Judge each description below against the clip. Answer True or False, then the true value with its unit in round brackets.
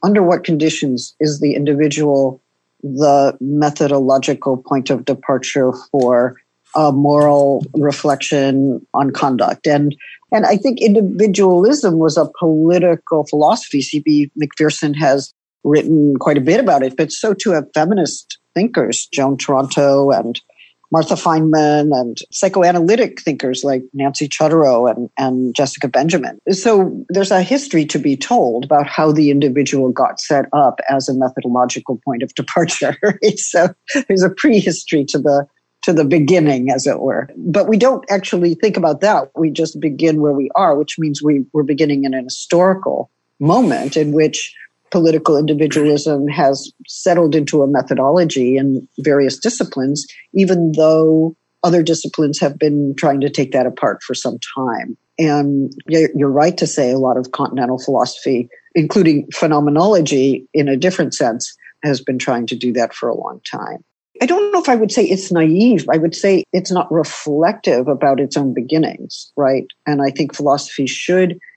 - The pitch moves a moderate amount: True (3.6 semitones)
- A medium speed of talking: True (155 wpm)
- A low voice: False (150 Hz)